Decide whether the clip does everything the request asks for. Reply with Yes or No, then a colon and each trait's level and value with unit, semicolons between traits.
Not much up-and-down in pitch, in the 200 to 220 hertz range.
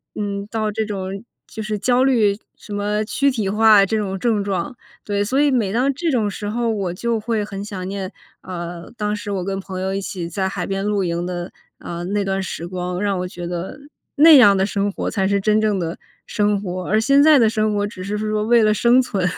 Yes: narrow, 2.3 semitones; high, 205 Hz